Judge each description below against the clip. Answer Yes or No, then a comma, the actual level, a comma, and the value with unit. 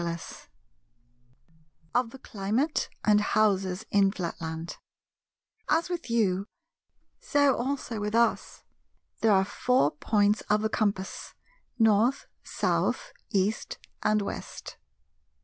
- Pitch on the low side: No, high, 210 Hz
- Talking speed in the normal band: No, slow, 110 wpm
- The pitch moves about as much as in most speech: Yes, average, 3.7 semitones